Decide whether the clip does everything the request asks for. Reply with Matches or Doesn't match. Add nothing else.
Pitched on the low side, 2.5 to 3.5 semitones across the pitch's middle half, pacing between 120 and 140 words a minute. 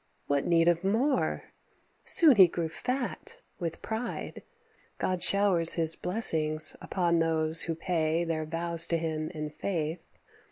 Doesn't match